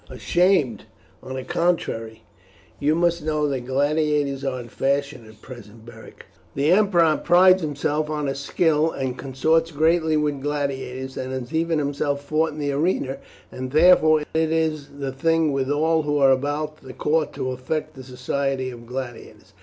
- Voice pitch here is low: No, medium, 145 Hz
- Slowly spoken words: No, average, 165 wpm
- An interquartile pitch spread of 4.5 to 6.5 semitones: No, average, 3.2 semitones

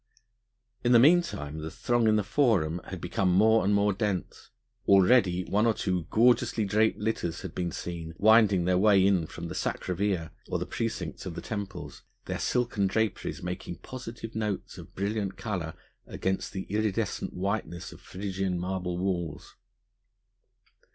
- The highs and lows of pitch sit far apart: No, average, 3.5 semitones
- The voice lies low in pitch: Yes, very low, 95 Hz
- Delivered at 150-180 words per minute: Yes, average, 160 wpm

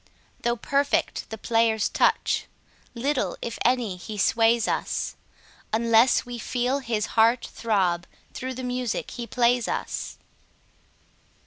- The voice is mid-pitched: No, high, 235 Hz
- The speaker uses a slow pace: Yes, slow, 120 wpm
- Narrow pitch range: Yes, narrow, 2.0 semitones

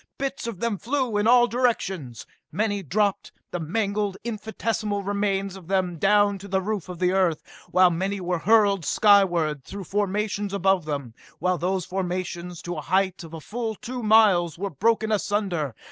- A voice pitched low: No, high, 195 Hz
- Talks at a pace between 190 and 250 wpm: No, average, 165 wpm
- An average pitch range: Yes, average, 3.0 semitones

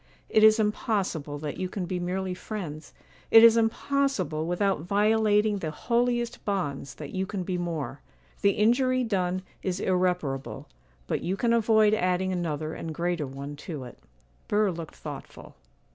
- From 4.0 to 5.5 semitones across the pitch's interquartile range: Yes, average, 4.9 semitones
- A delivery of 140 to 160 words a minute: Yes, average, 150 wpm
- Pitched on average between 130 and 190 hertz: Yes, medium, 185 Hz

